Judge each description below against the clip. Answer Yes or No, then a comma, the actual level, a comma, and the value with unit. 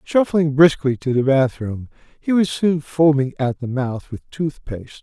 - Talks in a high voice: No, medium, 140 Hz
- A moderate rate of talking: Yes, average, 180 wpm